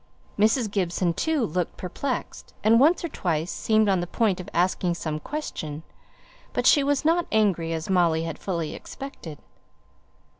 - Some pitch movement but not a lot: No, wide, 5.9 semitones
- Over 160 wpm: No, average, 155 wpm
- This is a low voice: No, medium, 185 Hz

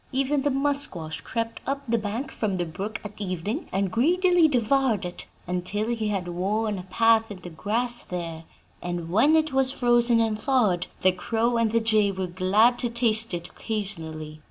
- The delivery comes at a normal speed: Yes, average, 180 wpm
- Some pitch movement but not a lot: Yes, average, 4.7 semitones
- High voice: Yes, high, 220 Hz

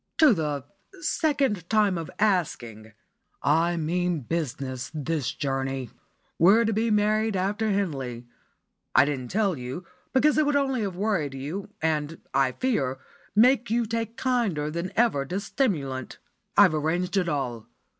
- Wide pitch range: Yes, wide, 7.6 semitones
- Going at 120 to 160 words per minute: Yes, average, 145 wpm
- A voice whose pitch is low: No, medium, 175 Hz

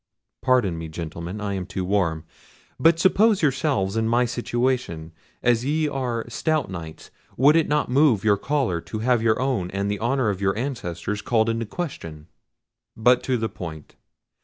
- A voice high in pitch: No, low, 115 Hz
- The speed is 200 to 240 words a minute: No, average, 170 wpm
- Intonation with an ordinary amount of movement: No, wide, 5.7 semitones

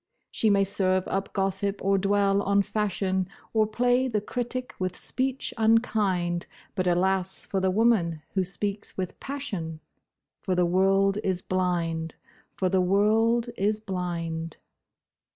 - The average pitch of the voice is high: Yes, high, 195 Hz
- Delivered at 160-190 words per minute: No, slow, 135 wpm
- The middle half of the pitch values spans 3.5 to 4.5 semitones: No, average, 2.8 semitones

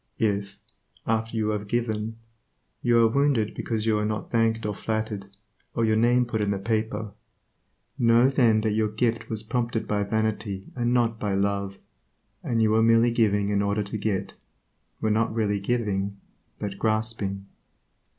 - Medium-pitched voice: No, low, 110 Hz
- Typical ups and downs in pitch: No, narrow, 1.9 semitones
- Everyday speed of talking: Yes, average, 165 wpm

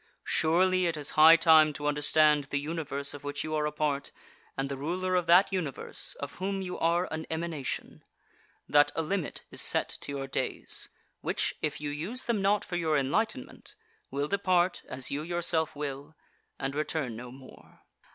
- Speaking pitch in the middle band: Yes, medium, 155 Hz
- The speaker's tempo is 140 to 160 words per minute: No, average, 180 wpm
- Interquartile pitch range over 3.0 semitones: Yes, average, 3.4 semitones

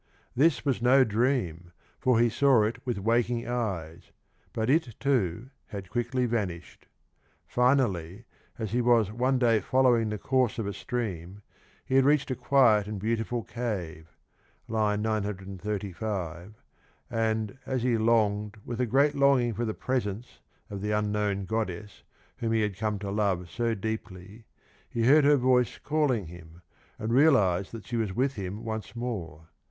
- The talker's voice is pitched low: Yes, low, 110 Hz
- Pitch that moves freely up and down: No, average, 3.6 semitones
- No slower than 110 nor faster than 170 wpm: Yes, average, 155 wpm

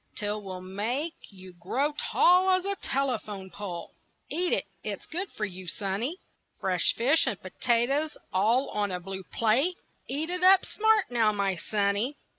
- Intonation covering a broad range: Yes, wide, 7.8 semitones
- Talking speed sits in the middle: Yes, average, 160 wpm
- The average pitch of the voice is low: No, high, 225 Hz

